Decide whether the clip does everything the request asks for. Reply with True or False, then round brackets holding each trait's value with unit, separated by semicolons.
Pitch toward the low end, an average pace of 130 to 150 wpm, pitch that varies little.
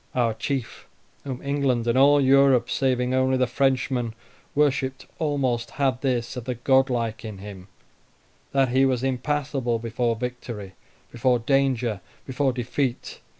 True (130 Hz; 135 wpm; 2.3 semitones)